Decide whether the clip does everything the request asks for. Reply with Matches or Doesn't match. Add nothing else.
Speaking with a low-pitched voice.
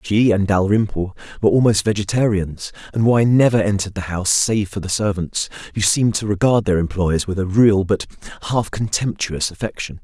Matches